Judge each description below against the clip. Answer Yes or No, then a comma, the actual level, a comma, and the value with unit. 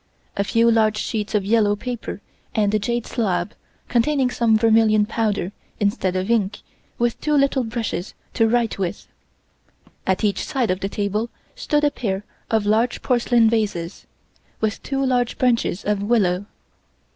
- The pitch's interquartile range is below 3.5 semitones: Yes, average, 2.8 semitones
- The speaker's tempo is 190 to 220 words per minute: No, average, 155 wpm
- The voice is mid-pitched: No, high, 220 Hz